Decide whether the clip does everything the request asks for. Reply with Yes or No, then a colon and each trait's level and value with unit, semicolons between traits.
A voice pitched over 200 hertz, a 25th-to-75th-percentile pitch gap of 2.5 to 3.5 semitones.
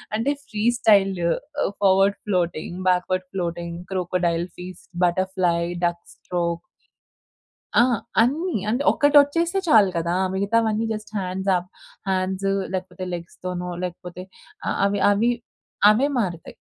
No: medium, 185 Hz; average, 3.2 semitones